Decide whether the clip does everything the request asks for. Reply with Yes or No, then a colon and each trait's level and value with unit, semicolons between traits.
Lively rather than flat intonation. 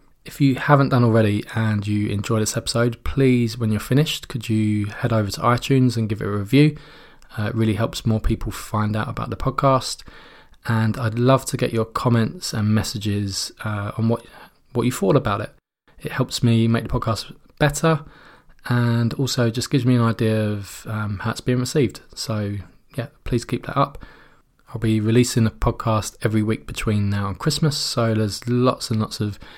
No: average, 2.8 semitones